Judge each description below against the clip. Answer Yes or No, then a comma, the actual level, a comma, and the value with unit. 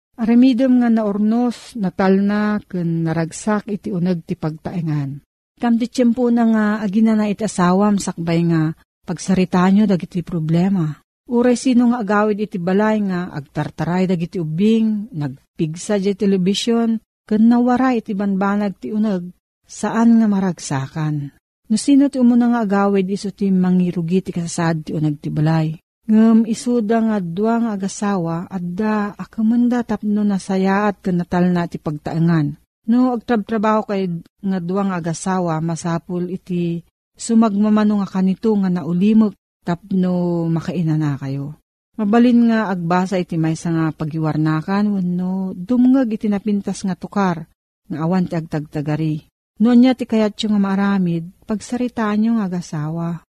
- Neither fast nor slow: Yes, average, 135 wpm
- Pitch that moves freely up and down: No, average, 4.1 semitones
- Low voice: No, high, 195 Hz